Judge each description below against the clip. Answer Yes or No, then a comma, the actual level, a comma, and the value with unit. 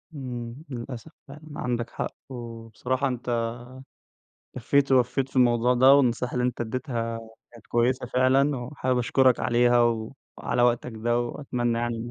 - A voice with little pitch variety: Yes, narrow, 1.6 semitones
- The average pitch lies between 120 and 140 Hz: Yes, low, 125 Hz